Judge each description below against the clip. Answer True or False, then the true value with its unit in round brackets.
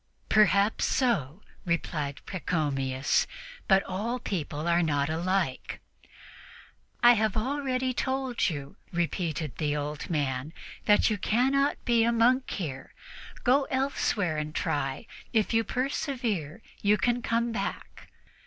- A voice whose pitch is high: True (195 Hz)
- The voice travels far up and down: True (7.9 semitones)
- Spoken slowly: True (120 wpm)